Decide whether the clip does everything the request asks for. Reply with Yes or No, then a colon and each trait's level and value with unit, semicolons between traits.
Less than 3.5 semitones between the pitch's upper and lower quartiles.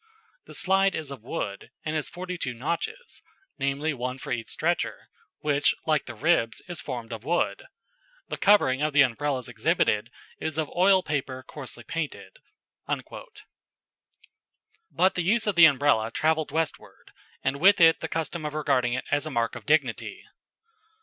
No: average, 4.7 semitones